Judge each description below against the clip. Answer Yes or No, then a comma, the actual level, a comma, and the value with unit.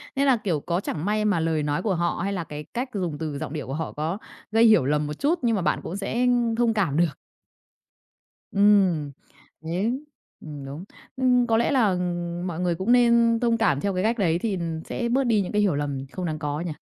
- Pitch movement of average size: No, wide, 6.1 semitones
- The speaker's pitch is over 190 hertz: No, medium, 185 Hz